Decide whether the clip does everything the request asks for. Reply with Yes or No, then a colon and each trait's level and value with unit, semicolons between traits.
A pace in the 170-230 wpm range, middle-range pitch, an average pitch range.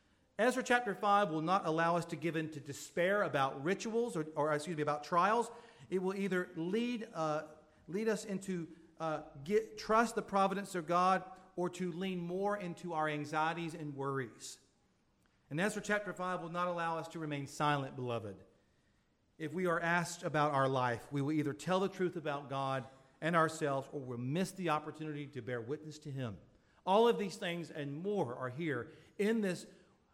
Yes: average, 185 wpm; medium, 165 Hz; average, 4.3 semitones